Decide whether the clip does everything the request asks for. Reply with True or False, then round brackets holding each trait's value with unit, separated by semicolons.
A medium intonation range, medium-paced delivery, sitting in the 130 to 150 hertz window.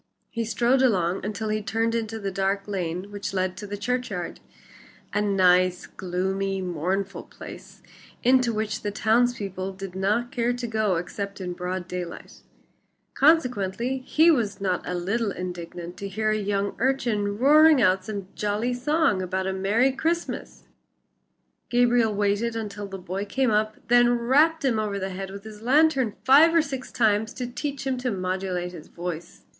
False (4.3 semitones; 165 wpm; 210 Hz)